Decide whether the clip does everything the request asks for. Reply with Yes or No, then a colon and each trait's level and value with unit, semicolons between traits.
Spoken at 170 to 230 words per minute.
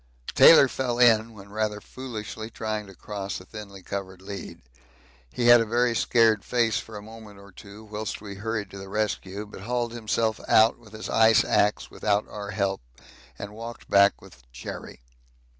Yes: average, 175 wpm